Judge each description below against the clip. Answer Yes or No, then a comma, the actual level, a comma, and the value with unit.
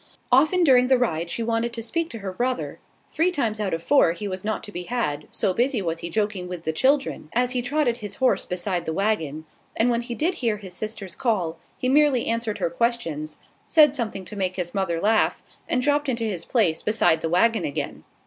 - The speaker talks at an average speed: No, fast, 220 wpm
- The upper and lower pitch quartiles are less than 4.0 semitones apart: No, wide, 5.6 semitones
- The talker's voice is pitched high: Yes, high, 220 Hz